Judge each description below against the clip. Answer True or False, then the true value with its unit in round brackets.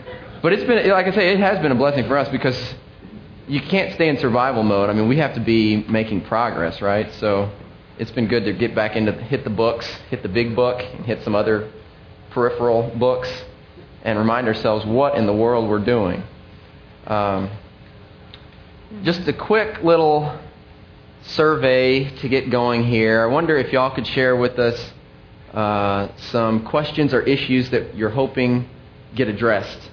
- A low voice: True (120 Hz)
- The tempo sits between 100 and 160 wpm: False (170 wpm)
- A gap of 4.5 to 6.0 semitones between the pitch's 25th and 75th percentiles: False (3.8 semitones)